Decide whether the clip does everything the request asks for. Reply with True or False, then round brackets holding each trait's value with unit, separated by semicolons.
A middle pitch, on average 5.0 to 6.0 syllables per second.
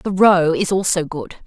False (175 Hz; 4.4 syllables/s)